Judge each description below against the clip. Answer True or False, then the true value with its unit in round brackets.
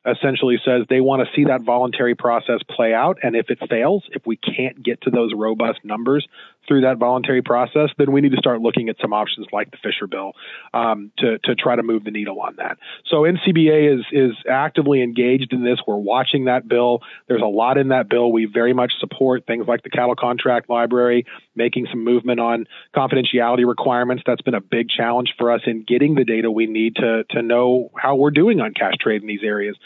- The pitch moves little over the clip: True (1.9 semitones)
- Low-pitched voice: True (120 Hz)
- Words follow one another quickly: True (220 wpm)